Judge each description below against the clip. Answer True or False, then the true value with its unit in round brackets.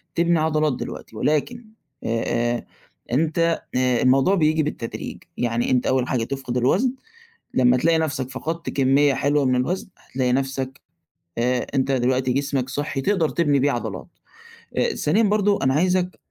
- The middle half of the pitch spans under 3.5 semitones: False (4.1 semitones)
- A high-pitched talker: False (135 Hz)